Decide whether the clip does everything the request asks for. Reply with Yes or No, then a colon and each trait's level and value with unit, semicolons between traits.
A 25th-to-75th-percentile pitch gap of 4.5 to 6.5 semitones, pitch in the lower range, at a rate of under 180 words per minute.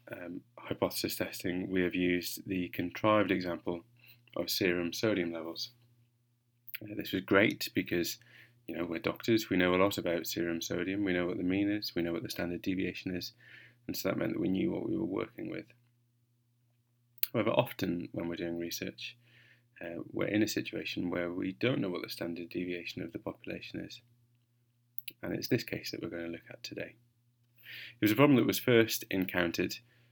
No: average, 5.2 semitones; low, 105 Hz; average, 190 wpm